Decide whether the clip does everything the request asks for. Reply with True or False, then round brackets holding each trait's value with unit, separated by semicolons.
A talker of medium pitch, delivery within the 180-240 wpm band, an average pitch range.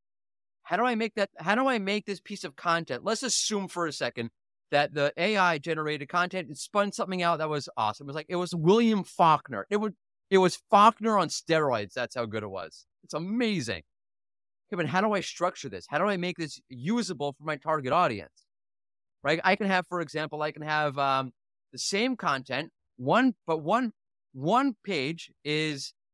False (170 Hz; 200 wpm; 5.7 semitones)